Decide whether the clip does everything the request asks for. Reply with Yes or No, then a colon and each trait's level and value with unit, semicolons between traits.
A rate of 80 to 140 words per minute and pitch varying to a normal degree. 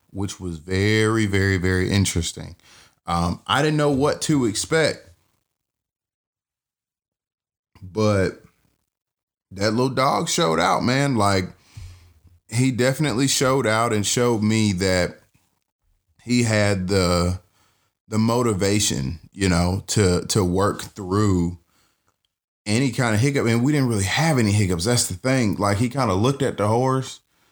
Yes: slow, 135 wpm; average, 4.6 semitones